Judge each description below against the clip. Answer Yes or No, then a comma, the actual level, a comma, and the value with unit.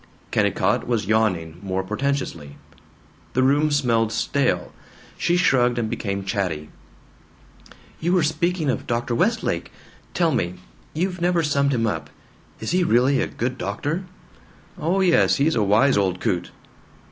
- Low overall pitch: Yes, low, 125 Hz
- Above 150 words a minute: No, average, 140 wpm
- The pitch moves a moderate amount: No, wide, 7.5 semitones